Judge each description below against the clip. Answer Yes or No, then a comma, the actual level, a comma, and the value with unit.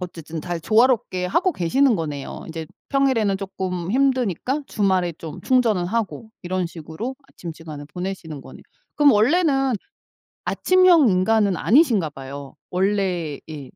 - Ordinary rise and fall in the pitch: No, wide, 7.2 semitones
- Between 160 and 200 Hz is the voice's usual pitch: Yes, high, 190 Hz